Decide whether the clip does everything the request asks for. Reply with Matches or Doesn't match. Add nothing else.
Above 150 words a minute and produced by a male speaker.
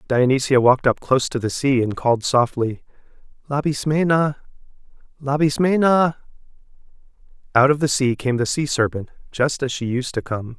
Doesn't match